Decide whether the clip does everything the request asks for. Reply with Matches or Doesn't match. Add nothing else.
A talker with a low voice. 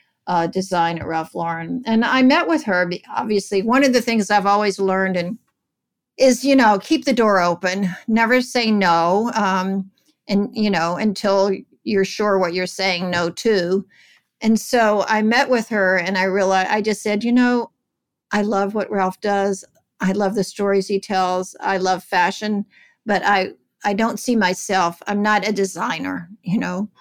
Doesn't match